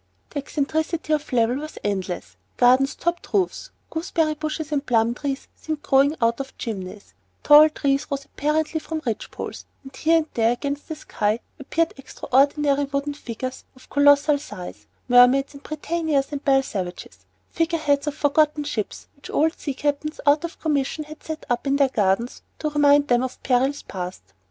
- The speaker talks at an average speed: Yes, average, 170 wpm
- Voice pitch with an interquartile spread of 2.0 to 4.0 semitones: Yes, average, 3.3 semitones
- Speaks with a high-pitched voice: Yes, very high, 285 Hz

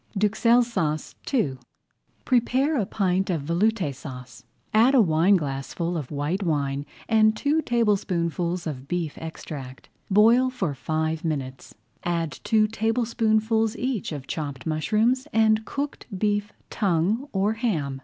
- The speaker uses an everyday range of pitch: No, wide, 6.1 semitones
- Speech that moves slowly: Yes, slow, 125 wpm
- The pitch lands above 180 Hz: Yes, high, 190 Hz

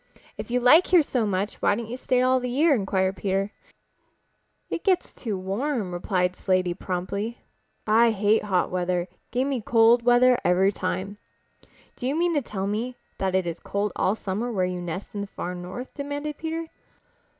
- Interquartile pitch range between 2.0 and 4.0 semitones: No, average, 5.0 semitones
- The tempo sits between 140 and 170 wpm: No, average, 185 wpm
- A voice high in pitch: Yes, high, 210 Hz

